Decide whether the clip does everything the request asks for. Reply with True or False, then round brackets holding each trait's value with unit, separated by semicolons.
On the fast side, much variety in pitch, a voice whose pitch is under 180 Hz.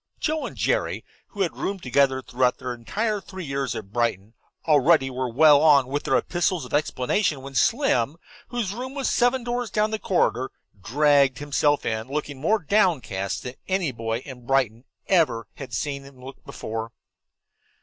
False (170 wpm; 7.0 semitones; 140 Hz)